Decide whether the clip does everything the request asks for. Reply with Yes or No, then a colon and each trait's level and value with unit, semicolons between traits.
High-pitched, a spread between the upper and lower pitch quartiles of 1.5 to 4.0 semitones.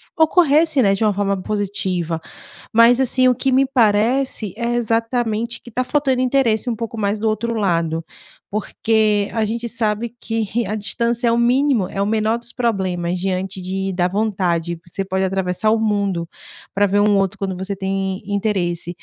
Yes: high, 215 Hz; average, 3.6 semitones